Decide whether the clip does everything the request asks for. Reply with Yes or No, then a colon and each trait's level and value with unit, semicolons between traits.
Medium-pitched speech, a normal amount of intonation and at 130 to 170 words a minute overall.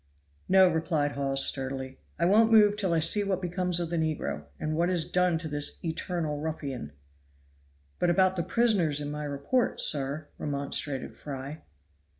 Yes: medium, 160 Hz; average, 3.9 semitones; average, 160 wpm